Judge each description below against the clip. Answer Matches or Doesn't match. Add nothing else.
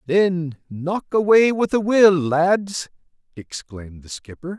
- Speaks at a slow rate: Matches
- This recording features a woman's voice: Doesn't match